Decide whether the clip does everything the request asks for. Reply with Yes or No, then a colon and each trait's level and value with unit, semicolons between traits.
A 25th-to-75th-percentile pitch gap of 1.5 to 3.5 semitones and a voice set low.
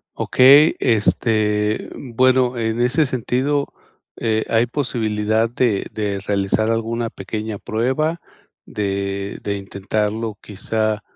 Yes: average, 2.9 semitones; low, 110 Hz